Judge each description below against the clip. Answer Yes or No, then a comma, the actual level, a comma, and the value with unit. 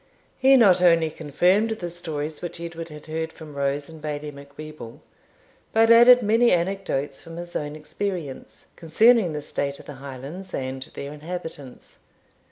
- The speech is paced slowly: No, average, 155 wpm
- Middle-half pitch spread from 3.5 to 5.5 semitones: Yes, average, 3.8 semitones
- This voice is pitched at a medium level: Yes, medium, 160 Hz